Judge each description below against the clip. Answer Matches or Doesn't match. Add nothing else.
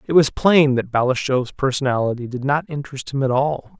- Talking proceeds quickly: Doesn't match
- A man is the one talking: Matches